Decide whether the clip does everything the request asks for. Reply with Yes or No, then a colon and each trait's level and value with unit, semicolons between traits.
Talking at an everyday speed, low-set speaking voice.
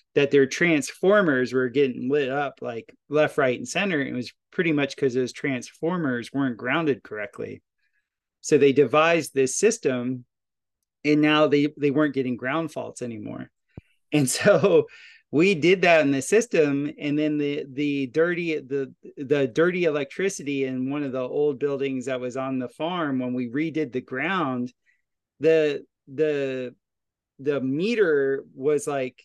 No: average, 155 wpm; medium, 145 Hz